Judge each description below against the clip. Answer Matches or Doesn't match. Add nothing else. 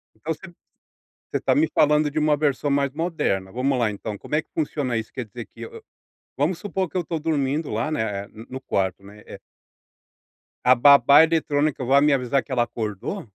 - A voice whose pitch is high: Doesn't match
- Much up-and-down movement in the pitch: Doesn't match